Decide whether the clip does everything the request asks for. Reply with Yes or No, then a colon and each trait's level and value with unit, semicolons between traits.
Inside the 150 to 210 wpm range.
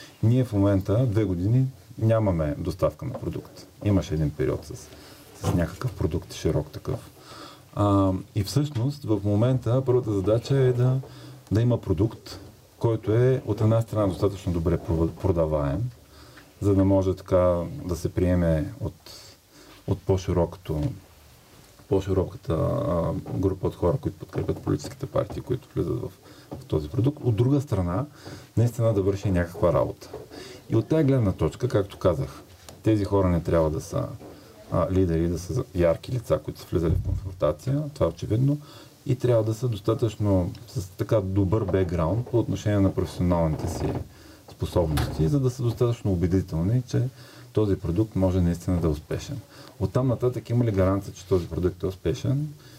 Yes: average, 155 wpm